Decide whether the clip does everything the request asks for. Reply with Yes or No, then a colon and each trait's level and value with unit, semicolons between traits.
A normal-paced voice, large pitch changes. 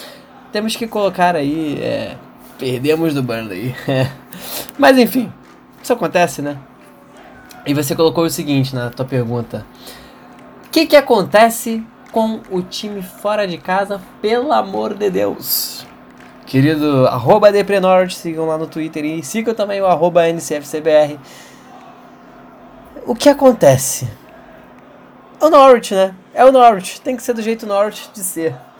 Yes: average, 140 wpm; wide, 6.9 semitones